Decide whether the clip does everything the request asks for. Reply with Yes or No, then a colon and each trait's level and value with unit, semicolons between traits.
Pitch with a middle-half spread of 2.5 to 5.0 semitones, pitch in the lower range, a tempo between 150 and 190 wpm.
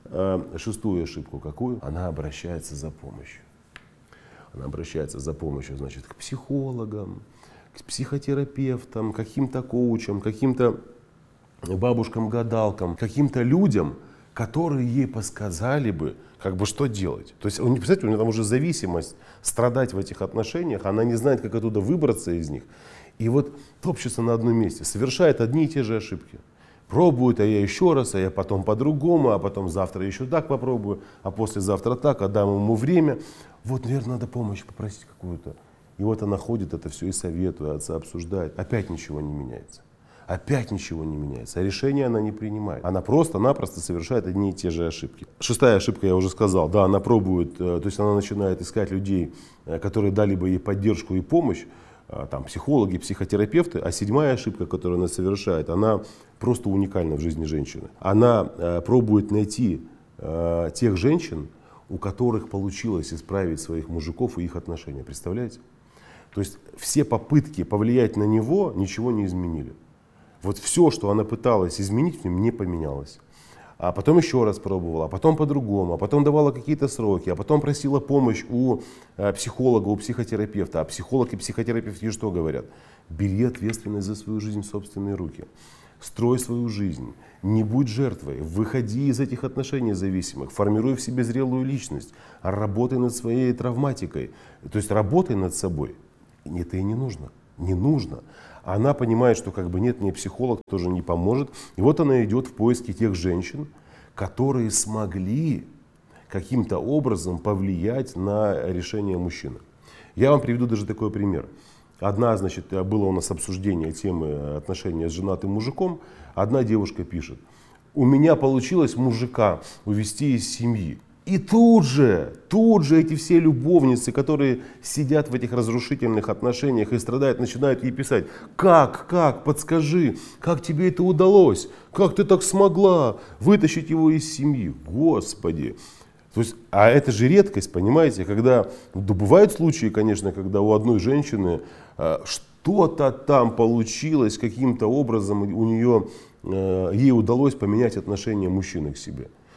No: wide, 5.4 semitones; low, 110 Hz; average, 155 wpm